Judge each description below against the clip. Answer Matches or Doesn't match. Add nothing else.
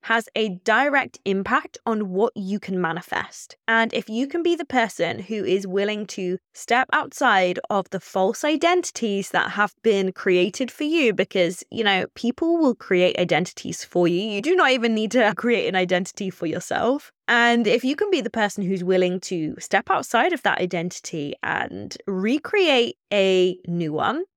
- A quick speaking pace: Doesn't match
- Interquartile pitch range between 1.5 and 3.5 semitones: Doesn't match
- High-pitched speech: Matches